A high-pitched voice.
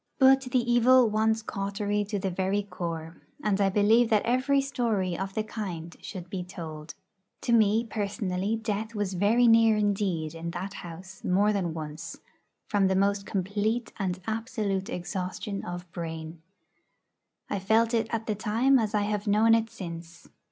Yes: high, 205 Hz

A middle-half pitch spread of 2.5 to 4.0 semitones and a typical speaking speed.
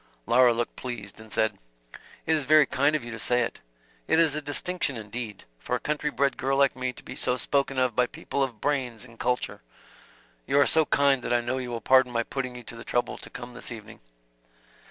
No: average, 2.9 semitones; fast, 230 wpm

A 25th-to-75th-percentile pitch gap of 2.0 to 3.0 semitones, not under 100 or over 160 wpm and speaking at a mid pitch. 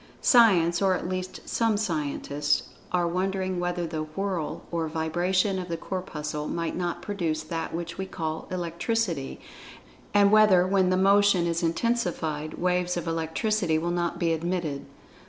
Yes: narrow, 2.6 semitones; average, 150 wpm; medium, 175 Hz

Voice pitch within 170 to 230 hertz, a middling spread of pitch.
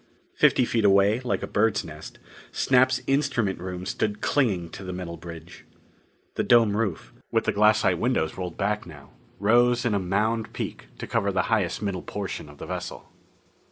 No: low, 100 Hz; average, 4.0 semitones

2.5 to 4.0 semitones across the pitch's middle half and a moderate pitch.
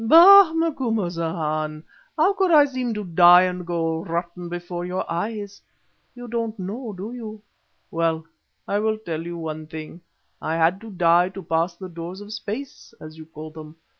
No: average, 5.0 semitones; medium, 180 Hz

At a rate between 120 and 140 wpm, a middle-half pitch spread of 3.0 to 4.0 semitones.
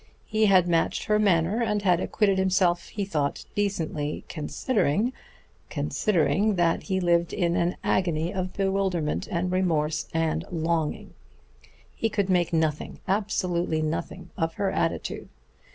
Yes: slow, 135 wpm; average, 3.3 semitones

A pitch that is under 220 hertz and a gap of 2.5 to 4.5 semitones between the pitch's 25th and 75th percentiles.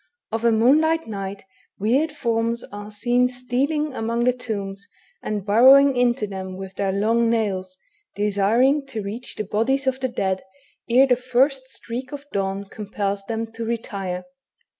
No: high, 230 Hz; average, 4.1 semitones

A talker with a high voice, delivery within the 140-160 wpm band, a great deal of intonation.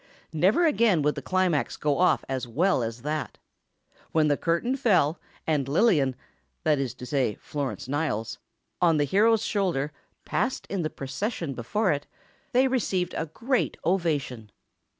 No: medium, 155 Hz; average, 145 wpm; wide, 5.9 semitones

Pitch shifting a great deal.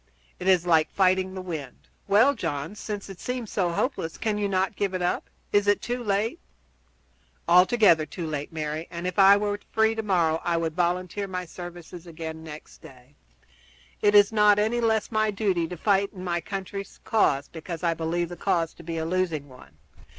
No: average, 3.8 semitones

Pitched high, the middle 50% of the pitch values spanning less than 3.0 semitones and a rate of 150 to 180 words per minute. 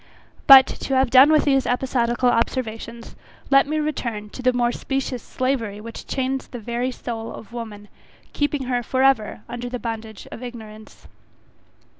Yes: high, 245 Hz; narrow, 2.5 semitones; average, 160 wpm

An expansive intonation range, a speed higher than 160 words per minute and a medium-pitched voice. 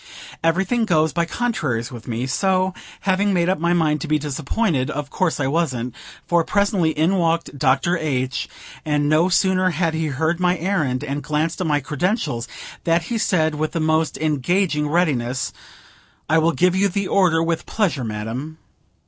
No: average, 3.8 semitones; average, 175 wpm; medium, 160 Hz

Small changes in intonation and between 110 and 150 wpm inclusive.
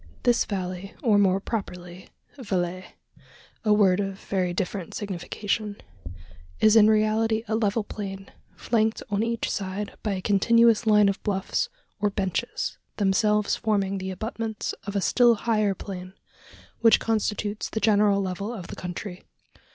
Yes: narrow, 2.2 semitones; average, 145 wpm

